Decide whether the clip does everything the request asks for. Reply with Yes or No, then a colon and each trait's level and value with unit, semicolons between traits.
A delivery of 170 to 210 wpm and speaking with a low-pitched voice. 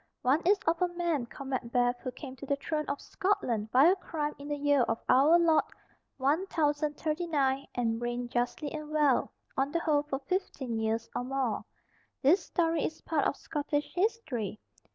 No: average, 175 wpm; very high, 290 Hz